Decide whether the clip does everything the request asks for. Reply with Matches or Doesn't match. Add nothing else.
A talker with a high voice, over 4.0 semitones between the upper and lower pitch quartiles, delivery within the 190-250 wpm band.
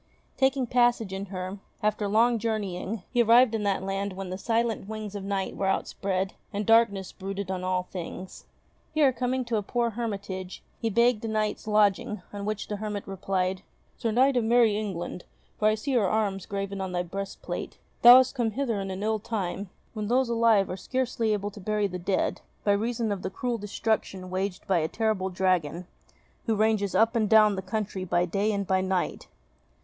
Doesn't match